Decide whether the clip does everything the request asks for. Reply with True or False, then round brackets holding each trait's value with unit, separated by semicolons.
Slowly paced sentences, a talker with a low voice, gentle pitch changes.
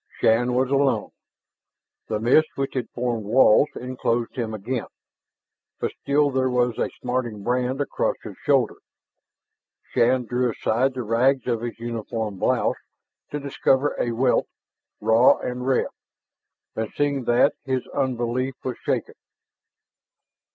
True (130 wpm; 125 Hz; 2.1 semitones)